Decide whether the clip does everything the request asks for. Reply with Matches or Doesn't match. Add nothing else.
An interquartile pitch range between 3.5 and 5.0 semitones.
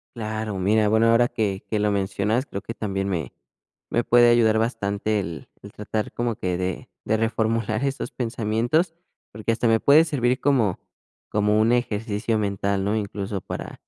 Doesn't match